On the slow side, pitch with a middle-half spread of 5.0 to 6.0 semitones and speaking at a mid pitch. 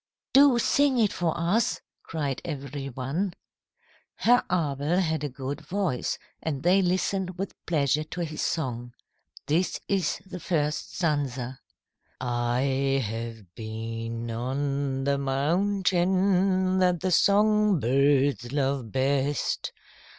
Yes: slow, 115 wpm; wide, 5.6 semitones; medium, 145 Hz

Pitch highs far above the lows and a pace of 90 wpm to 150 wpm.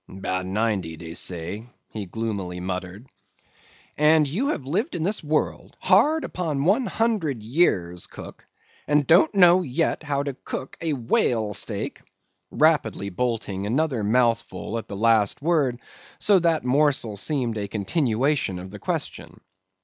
Yes: wide, 7.4 semitones; average, 140 wpm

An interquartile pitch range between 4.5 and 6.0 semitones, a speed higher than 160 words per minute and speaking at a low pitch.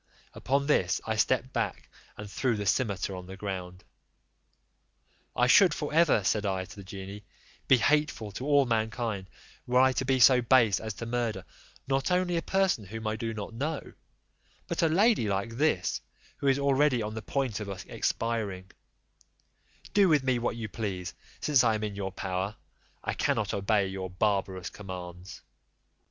Yes: average, 5.2 semitones; average, 170 wpm; low, 110 Hz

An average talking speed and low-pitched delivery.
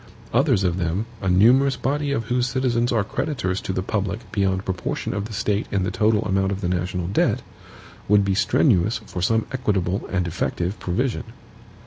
Yes: average, 180 wpm; low, 100 Hz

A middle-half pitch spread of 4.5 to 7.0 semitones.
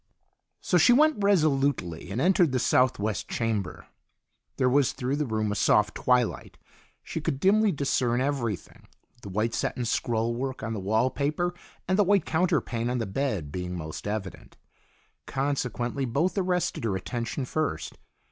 Yes: wide, 5.4 semitones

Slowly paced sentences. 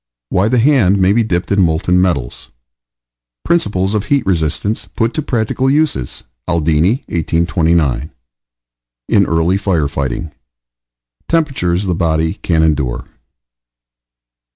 Yes: slow, 115 wpm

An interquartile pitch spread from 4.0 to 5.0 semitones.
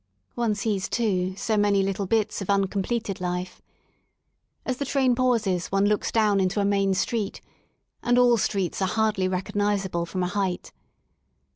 No: narrow, 2.6 semitones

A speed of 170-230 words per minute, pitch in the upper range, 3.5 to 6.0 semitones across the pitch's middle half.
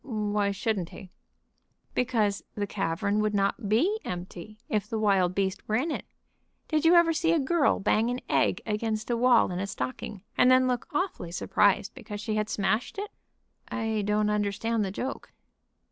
Yes: average, 175 wpm; high, 215 Hz; average, 3.9 semitones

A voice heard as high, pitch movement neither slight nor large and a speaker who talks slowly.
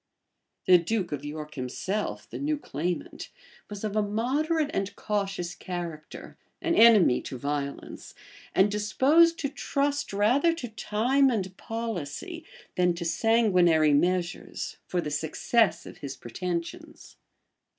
No: high, 200 Hz; wide, 6.0 semitones; slow, 130 wpm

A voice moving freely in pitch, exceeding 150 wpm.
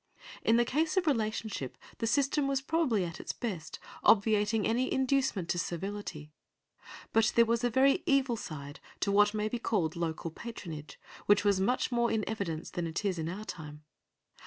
Yes: wide, 5.8 semitones; average, 180 wpm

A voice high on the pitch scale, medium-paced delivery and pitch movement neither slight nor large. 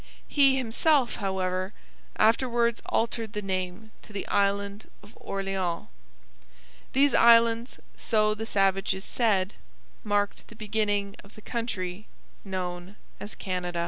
No: high, 205 Hz; slow, 115 wpm; average, 3.2 semitones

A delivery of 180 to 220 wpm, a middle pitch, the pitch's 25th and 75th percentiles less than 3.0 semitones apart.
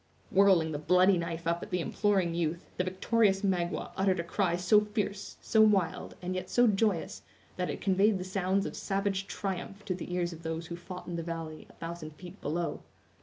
Yes: fast, 205 wpm; medium, 180 Hz; narrow, 2.5 semitones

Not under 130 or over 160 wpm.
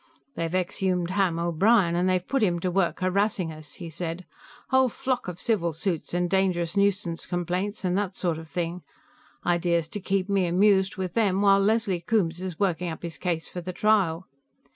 No: average, 185 wpm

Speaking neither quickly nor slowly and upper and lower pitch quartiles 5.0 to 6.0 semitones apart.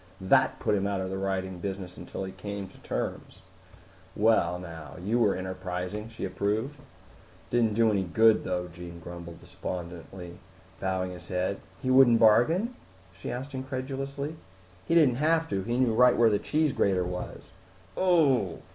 Yes: average, 165 wpm; wide, 5.5 semitones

